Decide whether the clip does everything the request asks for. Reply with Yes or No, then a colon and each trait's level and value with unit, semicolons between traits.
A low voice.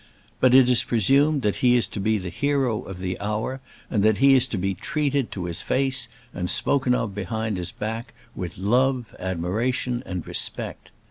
Yes: low, 115 Hz